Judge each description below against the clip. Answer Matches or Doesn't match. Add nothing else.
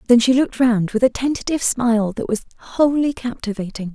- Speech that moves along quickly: Doesn't match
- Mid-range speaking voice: Doesn't match